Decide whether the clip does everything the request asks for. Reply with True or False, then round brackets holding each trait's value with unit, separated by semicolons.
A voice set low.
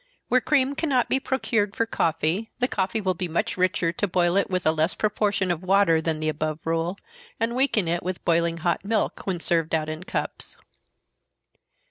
False (185 Hz)